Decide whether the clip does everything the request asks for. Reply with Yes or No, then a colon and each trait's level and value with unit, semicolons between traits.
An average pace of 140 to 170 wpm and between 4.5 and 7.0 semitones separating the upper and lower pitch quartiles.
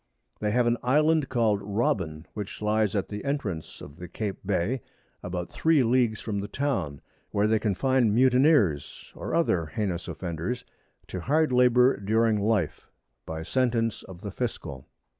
Yes: average, 155 wpm; average, 5.0 semitones